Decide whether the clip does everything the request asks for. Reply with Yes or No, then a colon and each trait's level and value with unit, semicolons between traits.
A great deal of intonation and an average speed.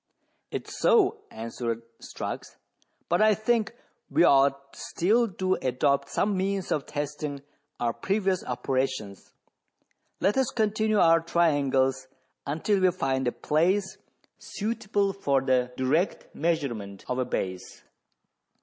No: wide, 7.1 semitones; slow, 120 wpm